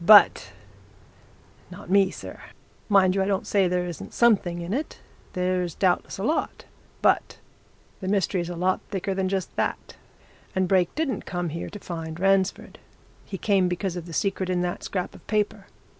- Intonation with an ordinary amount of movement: No, narrow, 1.9 semitones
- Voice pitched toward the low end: No, medium, 185 Hz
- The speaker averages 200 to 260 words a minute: No, average, 175 wpm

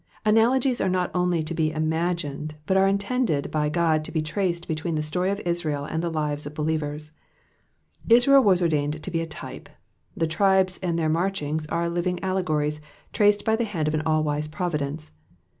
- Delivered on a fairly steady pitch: No, average, 3.5 semitones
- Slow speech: No, average, 195 wpm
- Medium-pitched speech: Yes, medium, 165 Hz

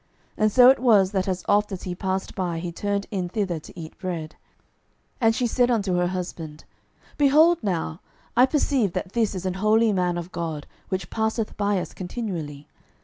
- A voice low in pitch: No, high, 190 Hz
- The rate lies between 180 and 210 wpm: Yes, average, 195 wpm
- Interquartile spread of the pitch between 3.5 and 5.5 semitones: Yes, average, 3.9 semitones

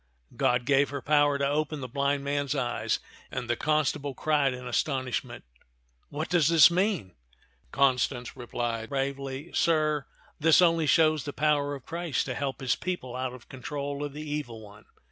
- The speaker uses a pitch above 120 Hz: Yes, medium, 140 Hz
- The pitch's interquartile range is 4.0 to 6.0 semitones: No, average, 3.1 semitones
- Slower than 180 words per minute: No, average, 185 wpm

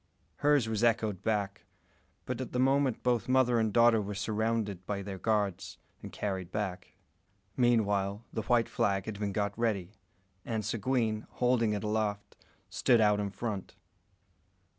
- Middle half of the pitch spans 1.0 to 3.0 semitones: Yes, narrow, 2.6 semitones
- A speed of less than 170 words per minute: Yes, average, 150 wpm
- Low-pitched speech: Yes, low, 110 Hz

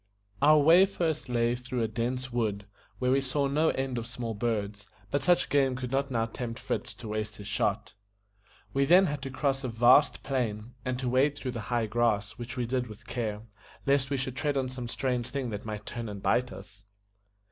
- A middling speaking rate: No, fast, 210 wpm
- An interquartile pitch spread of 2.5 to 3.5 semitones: Yes, average, 3.2 semitones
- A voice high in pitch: No, low, 125 Hz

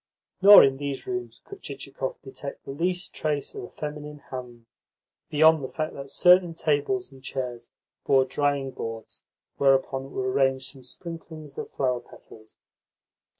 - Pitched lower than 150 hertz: Yes, medium, 140 Hz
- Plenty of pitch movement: No, average, 3.4 semitones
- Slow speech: No, average, 150 wpm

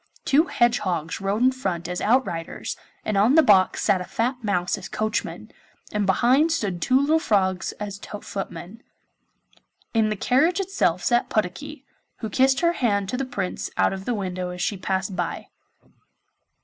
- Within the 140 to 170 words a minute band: Yes, average, 165 wpm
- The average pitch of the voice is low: No, high, 210 Hz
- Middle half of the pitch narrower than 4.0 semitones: No, wide, 5.5 semitones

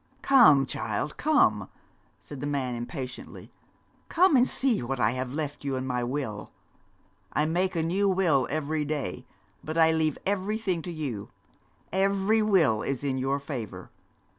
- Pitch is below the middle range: No, medium, 150 Hz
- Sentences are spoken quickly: No, average, 155 wpm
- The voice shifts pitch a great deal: Yes, wide, 6.4 semitones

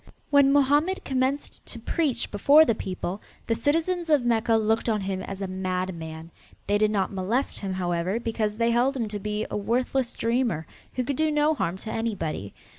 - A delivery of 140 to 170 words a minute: No, average, 190 wpm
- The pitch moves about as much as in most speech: No, wide, 5.9 semitones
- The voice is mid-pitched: No, high, 225 Hz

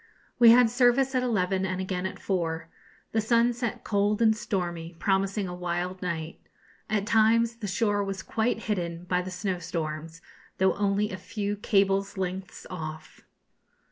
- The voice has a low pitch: No, high, 195 Hz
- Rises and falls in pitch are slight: No, average, 3.4 semitones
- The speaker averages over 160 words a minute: No, average, 155 wpm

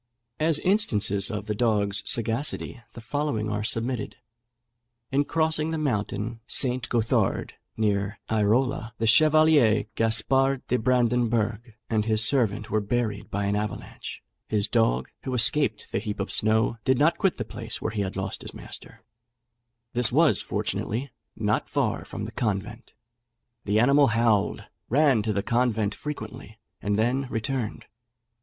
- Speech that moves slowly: No, average, 145 wpm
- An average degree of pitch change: Yes, average, 3.7 semitones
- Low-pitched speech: Yes, low, 115 Hz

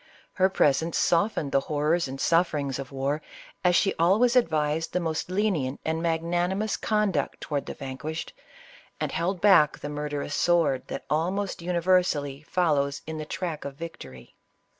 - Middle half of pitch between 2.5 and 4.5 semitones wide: Yes, average, 3.7 semitones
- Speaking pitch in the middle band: Yes, medium, 160 Hz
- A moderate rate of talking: Yes, average, 150 wpm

